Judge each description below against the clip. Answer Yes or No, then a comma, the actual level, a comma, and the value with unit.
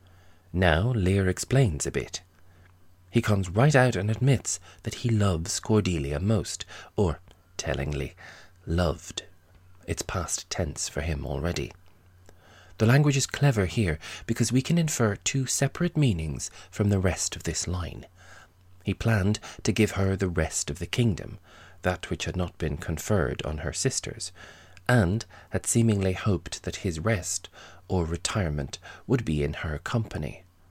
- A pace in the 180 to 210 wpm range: No, average, 150 wpm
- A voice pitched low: Yes, very low, 90 Hz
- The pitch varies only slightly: No, average, 4.2 semitones